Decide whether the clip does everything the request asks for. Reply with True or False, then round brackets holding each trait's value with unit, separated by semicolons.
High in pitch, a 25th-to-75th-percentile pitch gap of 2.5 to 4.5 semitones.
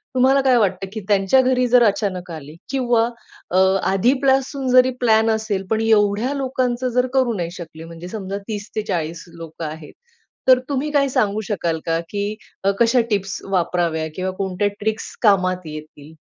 False (210 Hz; 5.6 semitones)